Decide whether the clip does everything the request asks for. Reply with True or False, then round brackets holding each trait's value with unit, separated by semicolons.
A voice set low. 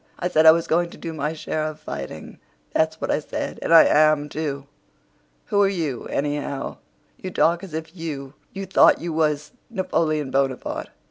False (155 Hz)